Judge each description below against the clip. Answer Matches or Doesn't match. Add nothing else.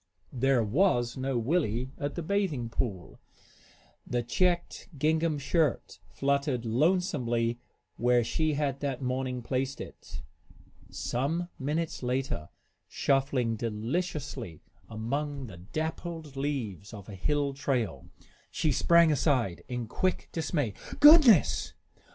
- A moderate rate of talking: Doesn't match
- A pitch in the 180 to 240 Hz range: Doesn't match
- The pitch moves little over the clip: Doesn't match